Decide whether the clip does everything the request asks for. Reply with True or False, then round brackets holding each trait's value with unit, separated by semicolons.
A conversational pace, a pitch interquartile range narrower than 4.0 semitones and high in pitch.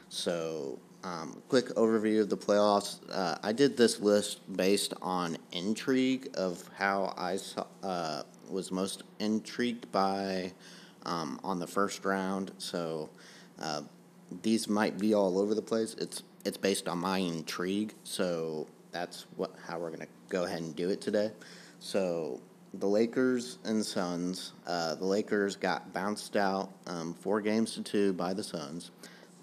False (155 wpm; 3.0 semitones; 100 Hz)